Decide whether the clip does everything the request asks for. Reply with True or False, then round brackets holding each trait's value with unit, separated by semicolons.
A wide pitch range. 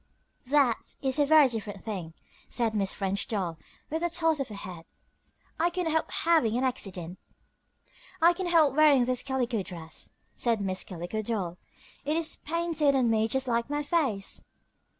True (7.3 semitones)